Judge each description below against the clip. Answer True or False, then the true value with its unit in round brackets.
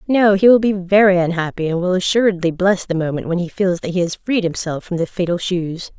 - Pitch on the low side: False (185 Hz)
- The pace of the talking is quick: True (240 wpm)